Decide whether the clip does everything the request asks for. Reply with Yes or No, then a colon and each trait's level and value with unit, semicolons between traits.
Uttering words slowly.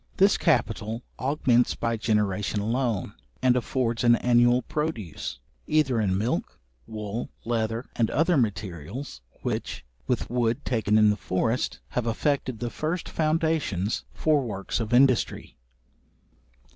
Yes: slow, 125 wpm